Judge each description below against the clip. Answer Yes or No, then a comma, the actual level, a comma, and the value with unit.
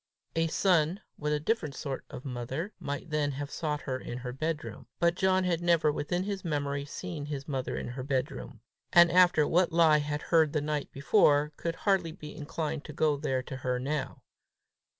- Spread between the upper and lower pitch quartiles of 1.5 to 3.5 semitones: Yes, average, 3.0 semitones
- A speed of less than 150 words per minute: No, average, 190 wpm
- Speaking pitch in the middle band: Yes, medium, 150 Hz